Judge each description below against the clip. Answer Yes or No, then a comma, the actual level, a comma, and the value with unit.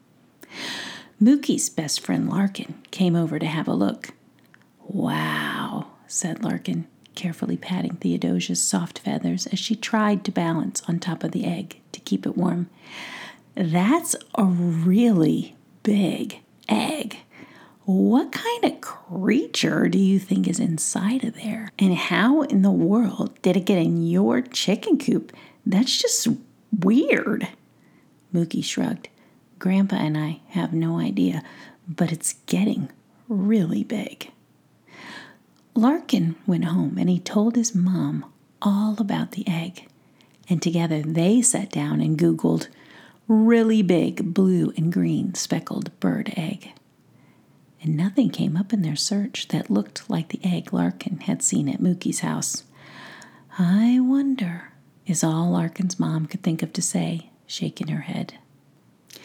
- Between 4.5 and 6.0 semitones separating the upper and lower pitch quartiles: Yes, average, 4.8 semitones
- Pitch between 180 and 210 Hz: Yes, high, 190 Hz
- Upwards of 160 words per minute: No, slow, 135 wpm